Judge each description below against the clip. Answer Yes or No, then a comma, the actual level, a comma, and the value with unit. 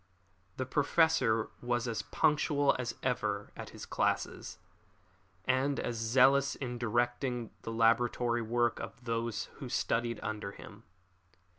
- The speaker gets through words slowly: Yes, slow, 125 wpm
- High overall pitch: No, low, 120 Hz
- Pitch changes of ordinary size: No, narrow, 2.2 semitones